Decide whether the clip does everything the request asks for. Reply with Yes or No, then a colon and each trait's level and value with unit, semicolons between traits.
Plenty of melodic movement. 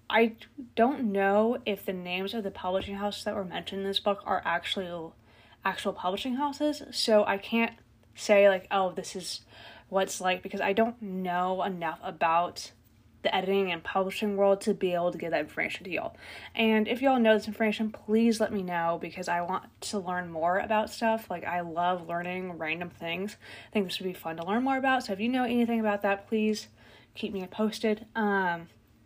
No: average, 3.5 semitones